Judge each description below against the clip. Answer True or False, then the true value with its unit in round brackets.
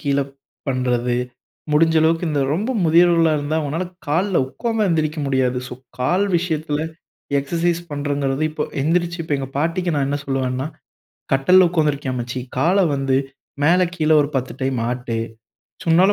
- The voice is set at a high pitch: False (150 Hz)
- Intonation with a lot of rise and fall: False (3.9 semitones)